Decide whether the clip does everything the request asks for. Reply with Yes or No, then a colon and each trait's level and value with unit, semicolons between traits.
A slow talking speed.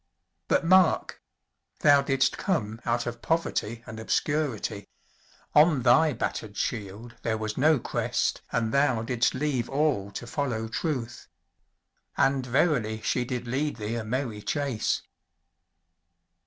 Yes: slow, 130 wpm